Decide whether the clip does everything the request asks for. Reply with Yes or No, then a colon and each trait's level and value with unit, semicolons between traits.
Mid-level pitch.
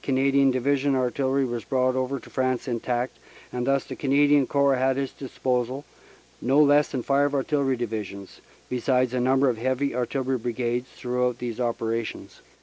No: low, 130 Hz